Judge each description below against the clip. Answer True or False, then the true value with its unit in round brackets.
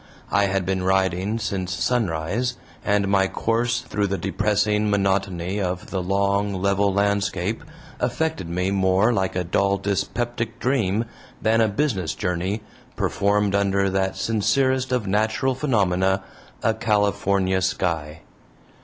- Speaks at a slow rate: True (125 wpm)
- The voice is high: False (100 Hz)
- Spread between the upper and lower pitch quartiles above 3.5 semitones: False (2.6 semitones)